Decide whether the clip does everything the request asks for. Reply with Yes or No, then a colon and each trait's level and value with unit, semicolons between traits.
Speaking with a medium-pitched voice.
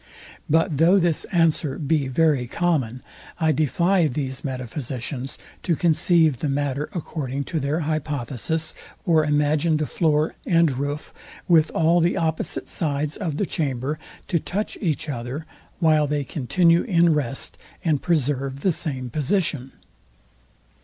Yes: medium, 150 Hz